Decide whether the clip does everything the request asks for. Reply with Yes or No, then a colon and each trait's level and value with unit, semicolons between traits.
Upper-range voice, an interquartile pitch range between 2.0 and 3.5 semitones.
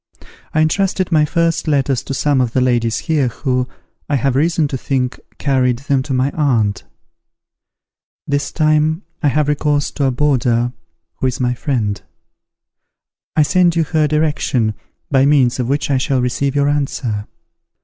No: medium, 140 Hz; average, 3.1 semitones